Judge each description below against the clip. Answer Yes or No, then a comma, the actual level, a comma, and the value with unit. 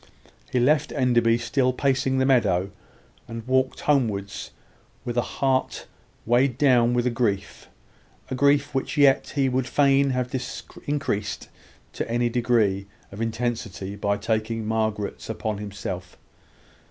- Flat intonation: No, average, 3.4 semitones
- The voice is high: No, low, 120 Hz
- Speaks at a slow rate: Yes, slow, 130 wpm